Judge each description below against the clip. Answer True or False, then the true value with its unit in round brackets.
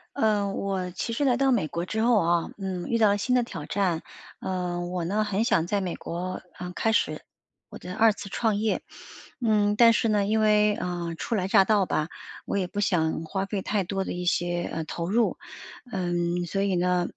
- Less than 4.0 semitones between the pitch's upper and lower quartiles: True (3.4 semitones)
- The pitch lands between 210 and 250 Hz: False (195 Hz)